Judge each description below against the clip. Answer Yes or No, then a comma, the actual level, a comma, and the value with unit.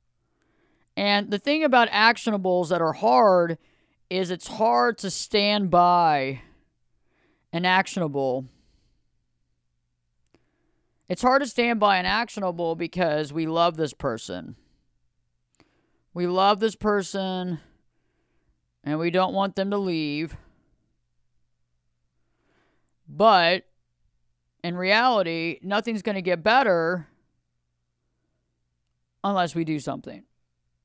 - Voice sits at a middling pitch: Yes, medium, 165 Hz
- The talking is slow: Yes, slow, 100 wpm